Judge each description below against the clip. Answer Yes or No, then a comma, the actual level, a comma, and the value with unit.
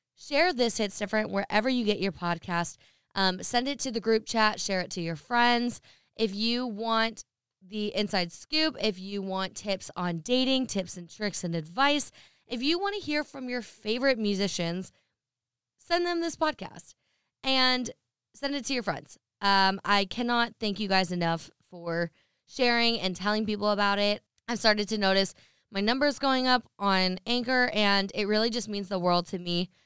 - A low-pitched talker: No, high, 210 Hz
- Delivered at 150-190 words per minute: Yes, average, 180 wpm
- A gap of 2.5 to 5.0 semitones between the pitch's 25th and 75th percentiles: Yes, average, 4.4 semitones